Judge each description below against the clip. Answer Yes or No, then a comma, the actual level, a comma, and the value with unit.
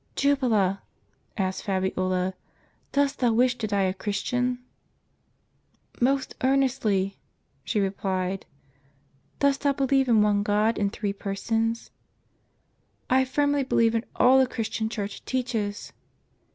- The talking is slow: Yes, slow, 125 wpm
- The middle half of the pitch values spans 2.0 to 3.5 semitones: No, average, 4.6 semitones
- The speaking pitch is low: No, high, 225 Hz